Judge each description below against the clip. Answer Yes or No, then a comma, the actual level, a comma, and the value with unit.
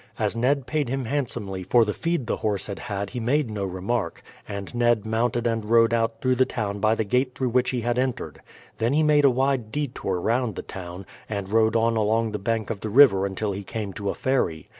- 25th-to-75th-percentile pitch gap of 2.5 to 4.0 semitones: Yes, average, 3.6 semitones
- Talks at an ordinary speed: No, fast, 230 wpm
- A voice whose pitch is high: No, low, 115 Hz